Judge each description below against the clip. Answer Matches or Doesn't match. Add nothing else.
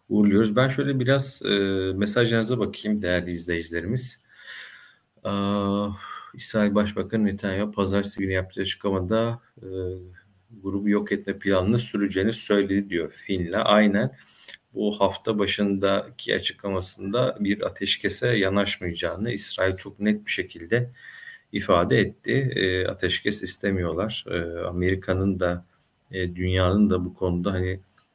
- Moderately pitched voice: Doesn't match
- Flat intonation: Matches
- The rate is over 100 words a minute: Matches